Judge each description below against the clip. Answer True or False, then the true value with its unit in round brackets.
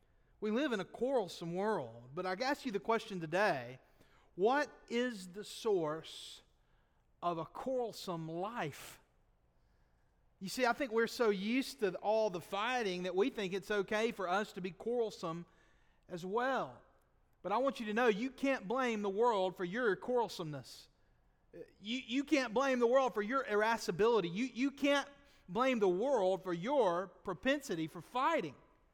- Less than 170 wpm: True (160 wpm)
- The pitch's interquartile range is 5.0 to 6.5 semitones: True (5.5 semitones)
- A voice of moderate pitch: False (215 Hz)